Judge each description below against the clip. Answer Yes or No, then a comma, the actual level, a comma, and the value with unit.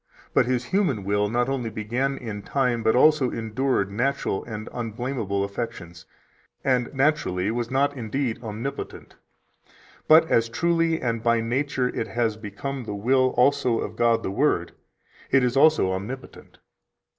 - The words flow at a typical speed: Yes, average, 145 wpm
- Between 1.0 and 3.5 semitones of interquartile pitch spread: No, average, 3.9 semitones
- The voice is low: Yes, low, 120 Hz